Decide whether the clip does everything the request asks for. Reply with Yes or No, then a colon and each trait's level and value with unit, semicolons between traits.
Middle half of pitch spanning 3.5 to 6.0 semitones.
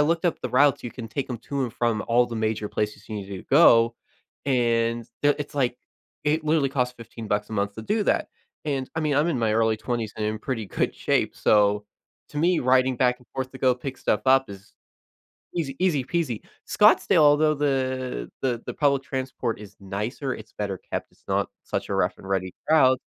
Yes: average, 4.2 semitones